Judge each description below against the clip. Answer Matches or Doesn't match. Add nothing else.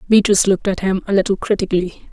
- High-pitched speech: Matches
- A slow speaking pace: Doesn't match